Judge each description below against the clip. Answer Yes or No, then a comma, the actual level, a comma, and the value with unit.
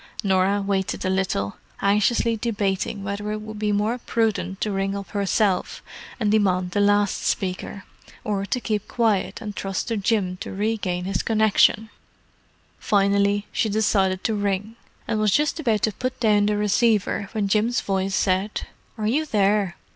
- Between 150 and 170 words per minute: Yes, average, 160 wpm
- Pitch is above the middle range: Yes, high, 205 Hz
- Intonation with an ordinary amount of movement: No, narrow, 1.9 semitones